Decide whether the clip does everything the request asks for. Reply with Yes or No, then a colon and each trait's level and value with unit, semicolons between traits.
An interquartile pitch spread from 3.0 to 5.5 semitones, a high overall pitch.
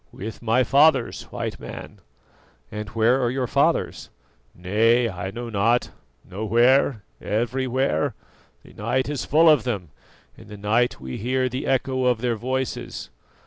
No: average, 3.4 semitones; low, 120 Hz